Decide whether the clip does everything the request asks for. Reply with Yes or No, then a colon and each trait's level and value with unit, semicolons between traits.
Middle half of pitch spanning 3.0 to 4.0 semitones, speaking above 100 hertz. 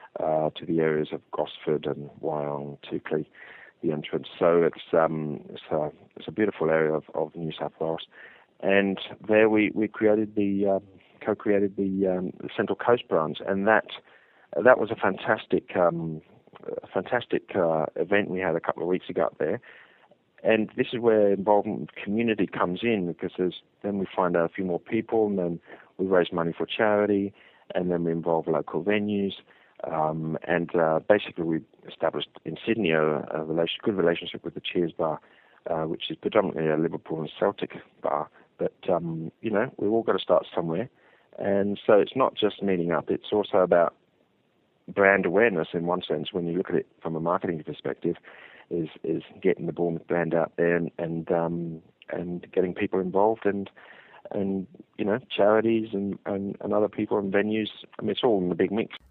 No: average, 3.7 semitones; very low, 90 Hz